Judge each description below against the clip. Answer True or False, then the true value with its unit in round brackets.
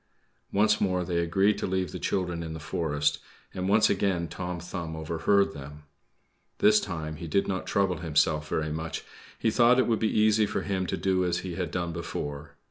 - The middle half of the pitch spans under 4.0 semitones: True (3.6 semitones)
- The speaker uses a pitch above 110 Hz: False (90 Hz)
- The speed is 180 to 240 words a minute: True (200 wpm)